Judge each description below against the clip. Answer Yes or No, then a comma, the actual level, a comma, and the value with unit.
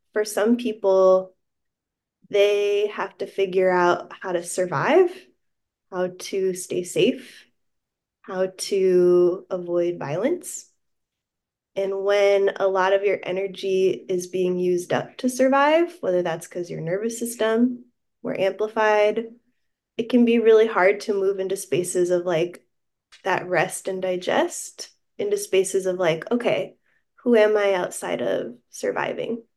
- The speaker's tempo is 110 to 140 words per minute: Yes, slow, 135 wpm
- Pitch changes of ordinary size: Yes, average, 3.8 semitones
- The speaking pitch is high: Yes, high, 195 Hz